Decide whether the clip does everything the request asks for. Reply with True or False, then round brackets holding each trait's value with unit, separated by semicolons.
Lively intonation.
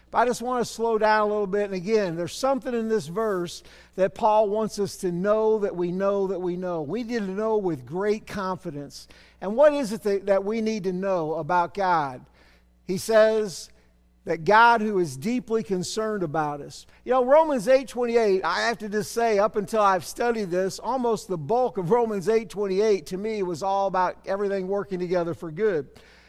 False (3.2 semitones)